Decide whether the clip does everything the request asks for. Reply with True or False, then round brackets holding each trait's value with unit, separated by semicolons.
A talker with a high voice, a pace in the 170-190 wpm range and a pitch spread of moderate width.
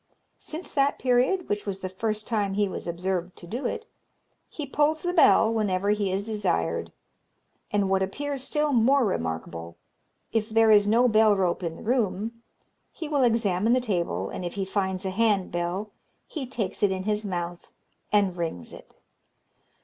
True (205 Hz; 175 wpm; 4.3 semitones)